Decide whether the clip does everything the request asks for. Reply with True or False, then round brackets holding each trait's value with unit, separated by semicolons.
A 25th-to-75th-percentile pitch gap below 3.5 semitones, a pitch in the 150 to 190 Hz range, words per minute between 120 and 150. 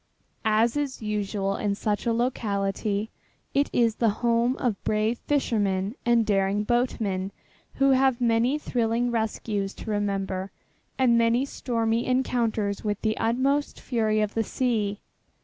False (2.9 semitones; 225 Hz; 135 wpm)